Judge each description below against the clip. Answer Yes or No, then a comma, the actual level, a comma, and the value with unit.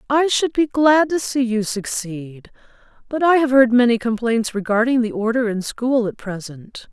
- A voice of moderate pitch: No, high, 240 Hz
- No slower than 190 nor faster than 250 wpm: No, average, 180 wpm